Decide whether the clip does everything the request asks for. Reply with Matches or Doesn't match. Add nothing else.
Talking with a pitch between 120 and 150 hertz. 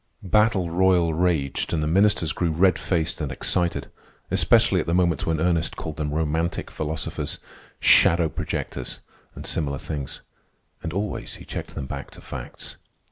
Doesn't match